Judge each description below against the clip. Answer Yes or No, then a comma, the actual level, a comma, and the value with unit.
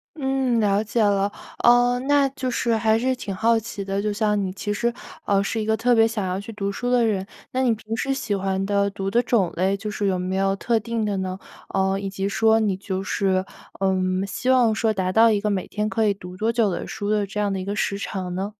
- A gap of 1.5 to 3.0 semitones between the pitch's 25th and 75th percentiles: Yes, average, 2.7 semitones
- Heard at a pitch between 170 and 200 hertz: No, high, 210 Hz